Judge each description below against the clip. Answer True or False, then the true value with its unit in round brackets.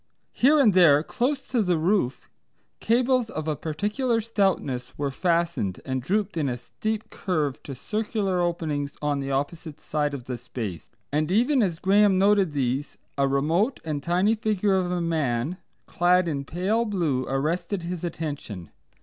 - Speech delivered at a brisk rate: False (160 wpm)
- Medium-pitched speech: True (170 Hz)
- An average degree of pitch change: False (6.3 semitones)